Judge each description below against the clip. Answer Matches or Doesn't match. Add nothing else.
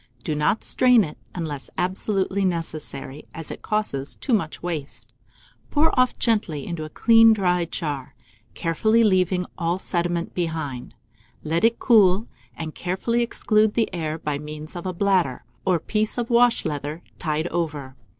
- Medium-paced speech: Matches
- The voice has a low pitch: Doesn't match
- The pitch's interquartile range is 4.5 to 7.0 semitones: Matches